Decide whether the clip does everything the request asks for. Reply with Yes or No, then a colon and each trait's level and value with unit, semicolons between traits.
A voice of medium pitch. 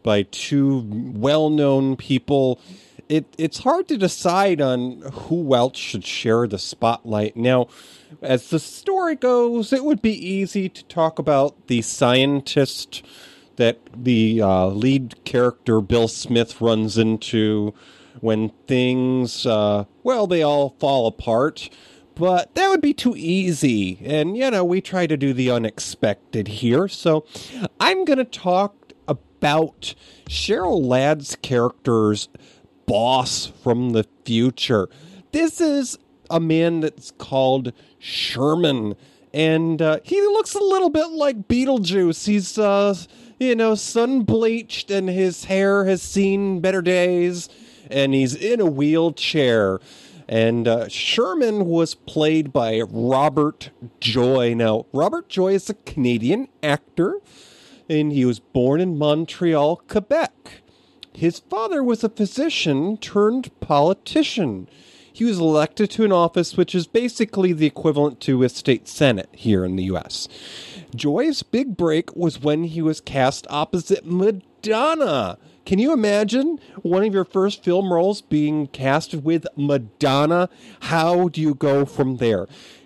Yes: medium, 155 Hz